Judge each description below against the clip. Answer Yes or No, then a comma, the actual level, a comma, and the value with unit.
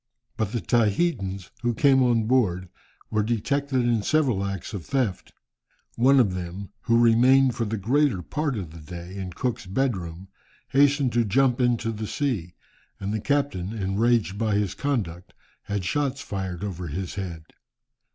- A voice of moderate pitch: No, low, 110 Hz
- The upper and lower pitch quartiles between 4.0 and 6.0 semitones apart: Yes, average, 5.2 semitones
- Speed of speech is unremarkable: Yes, average, 160 wpm